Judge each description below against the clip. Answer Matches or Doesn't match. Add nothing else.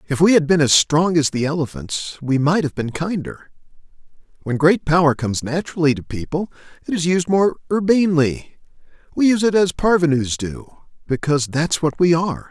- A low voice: Doesn't match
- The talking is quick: Doesn't match